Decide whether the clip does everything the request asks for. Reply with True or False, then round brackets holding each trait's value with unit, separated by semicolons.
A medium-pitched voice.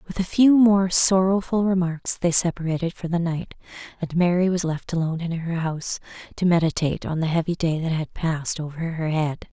True (170 Hz)